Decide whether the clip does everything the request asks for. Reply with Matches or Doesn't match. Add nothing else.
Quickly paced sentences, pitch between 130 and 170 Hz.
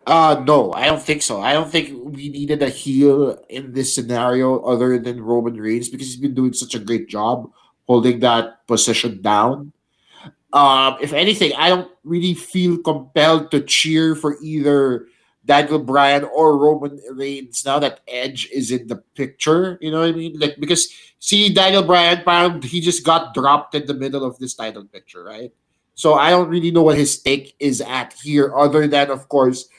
Doesn't match